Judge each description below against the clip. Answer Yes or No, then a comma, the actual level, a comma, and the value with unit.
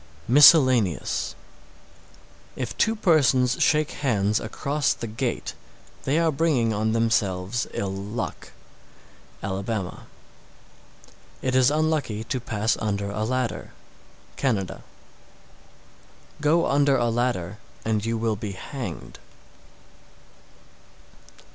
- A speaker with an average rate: No, slow, 110 wpm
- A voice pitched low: Yes, low, 115 Hz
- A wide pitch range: No, average, 4.7 semitones